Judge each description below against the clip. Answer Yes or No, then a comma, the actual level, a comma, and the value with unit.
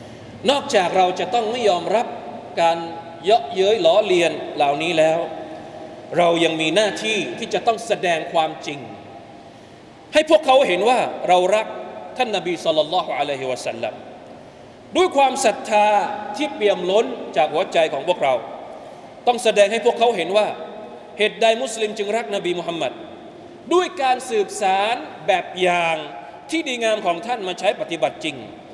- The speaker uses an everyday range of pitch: No, wide, 7.2 semitones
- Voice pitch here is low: No, high, 215 Hz